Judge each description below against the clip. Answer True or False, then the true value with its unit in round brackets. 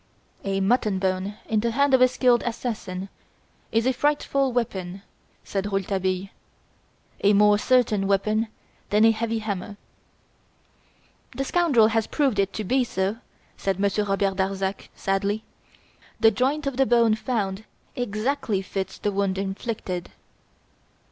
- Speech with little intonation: False (3.6 semitones)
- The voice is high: True (210 Hz)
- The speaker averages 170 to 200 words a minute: False (135 wpm)